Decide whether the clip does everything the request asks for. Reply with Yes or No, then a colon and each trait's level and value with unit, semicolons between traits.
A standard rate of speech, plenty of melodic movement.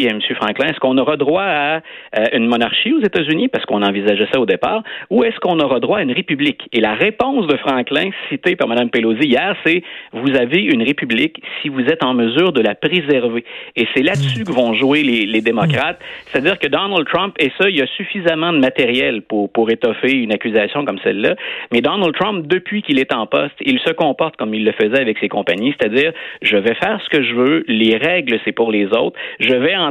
No: fast, 225 wpm; wide, 7.6 semitones